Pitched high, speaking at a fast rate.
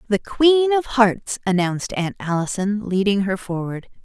No: high, 210 Hz; average, 150 wpm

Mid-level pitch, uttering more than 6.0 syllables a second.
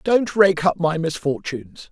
No: medium, 180 Hz; 4.4 syllables/s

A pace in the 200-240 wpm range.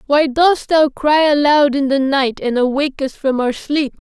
Yes: fast, 205 wpm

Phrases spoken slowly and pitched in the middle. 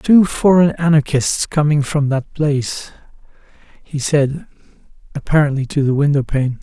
Yes: slow, 125 wpm; medium, 145 Hz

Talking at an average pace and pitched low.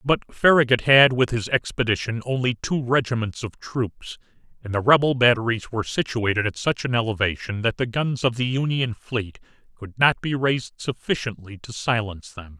Yes: average, 170 wpm; low, 120 Hz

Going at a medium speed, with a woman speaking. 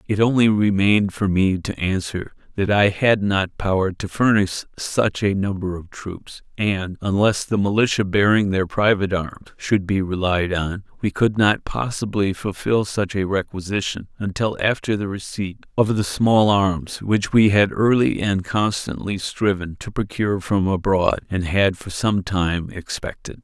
No: average, 165 wpm; male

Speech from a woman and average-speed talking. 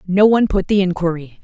No: female; fast, 210 wpm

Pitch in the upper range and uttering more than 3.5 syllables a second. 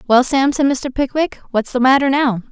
Yes: very high, 265 Hz; 5.1 syllables/s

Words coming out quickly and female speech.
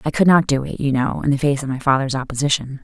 Yes: fast, 295 wpm; female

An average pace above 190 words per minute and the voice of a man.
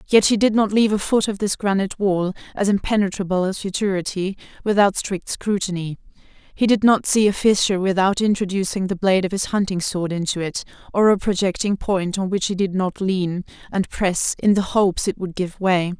No: average, 200 wpm; female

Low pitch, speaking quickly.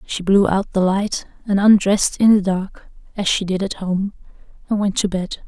No: high, 195 Hz; fast, 210 wpm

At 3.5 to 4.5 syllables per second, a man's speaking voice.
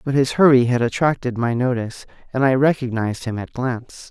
No: 5.9 syllables/s; male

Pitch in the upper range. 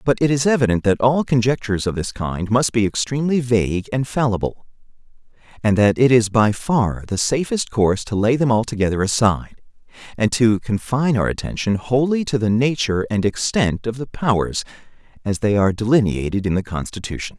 No: low, 115 Hz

